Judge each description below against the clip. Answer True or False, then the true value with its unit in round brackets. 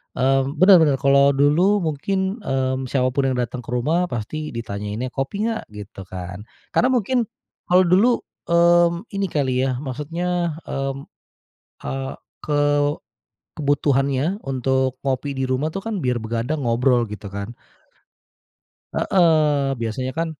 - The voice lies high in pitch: False (140 Hz)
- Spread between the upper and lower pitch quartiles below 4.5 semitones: False (5.0 semitones)